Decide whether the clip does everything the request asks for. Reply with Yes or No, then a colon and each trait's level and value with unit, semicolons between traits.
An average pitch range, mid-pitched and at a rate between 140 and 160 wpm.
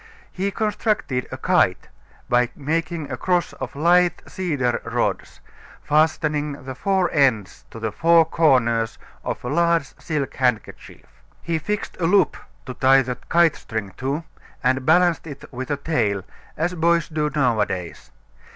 Yes: average, 4.9 semitones; medium, 150 Hz; average, 145 wpm